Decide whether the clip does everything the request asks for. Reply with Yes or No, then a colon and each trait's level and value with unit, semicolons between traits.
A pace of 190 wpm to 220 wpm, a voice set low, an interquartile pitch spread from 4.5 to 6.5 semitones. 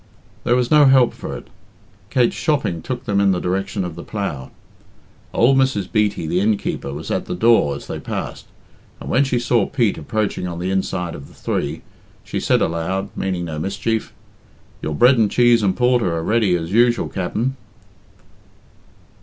No: average, 180 wpm; low, 100 Hz; wide, 5.4 semitones